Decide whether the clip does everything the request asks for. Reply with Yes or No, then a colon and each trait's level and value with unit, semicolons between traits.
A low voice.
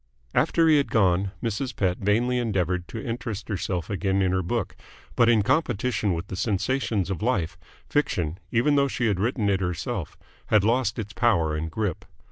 Yes: low, 105 Hz